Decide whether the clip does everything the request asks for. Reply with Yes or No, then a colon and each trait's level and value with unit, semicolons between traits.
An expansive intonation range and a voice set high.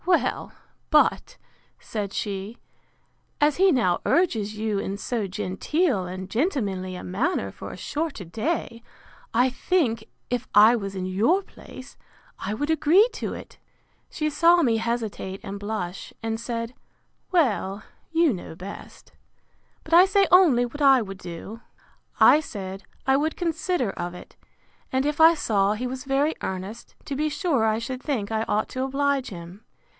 Yes: wide, 7.0 semitones; high, 235 Hz